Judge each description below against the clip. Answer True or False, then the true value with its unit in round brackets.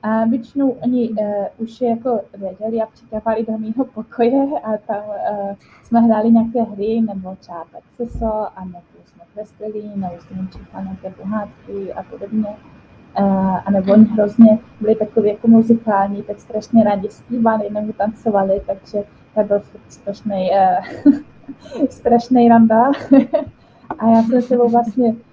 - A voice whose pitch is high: True (220 Hz)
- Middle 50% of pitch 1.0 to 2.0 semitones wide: False (2.5 semitones)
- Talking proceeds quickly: False (135 wpm)